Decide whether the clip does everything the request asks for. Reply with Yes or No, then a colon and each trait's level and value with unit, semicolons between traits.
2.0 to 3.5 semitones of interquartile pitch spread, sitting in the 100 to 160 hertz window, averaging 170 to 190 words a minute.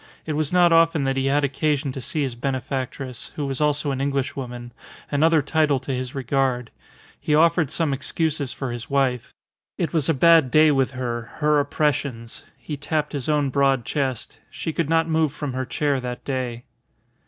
Yes: average, 2.8 semitones; medium, 140 Hz; average, 185 wpm